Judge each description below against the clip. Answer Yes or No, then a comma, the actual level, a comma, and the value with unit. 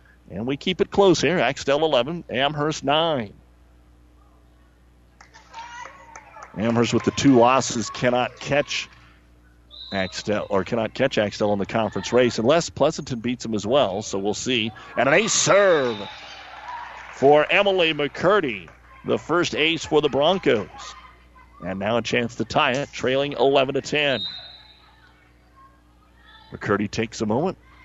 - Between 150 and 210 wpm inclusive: No, slow, 135 wpm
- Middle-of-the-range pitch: No, low, 115 Hz